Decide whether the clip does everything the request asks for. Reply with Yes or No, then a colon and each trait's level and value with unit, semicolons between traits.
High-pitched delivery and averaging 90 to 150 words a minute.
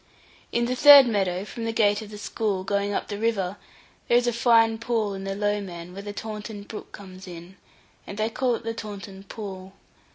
No: high, 205 Hz; fast, 205 wpm